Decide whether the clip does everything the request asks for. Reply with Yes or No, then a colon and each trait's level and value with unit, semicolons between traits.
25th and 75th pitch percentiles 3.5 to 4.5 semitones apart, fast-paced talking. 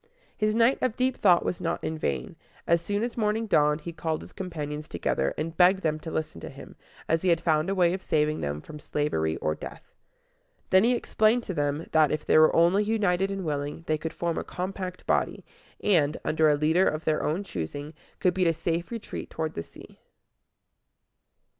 Yes: average, 4.0 semitones; fast, 210 wpm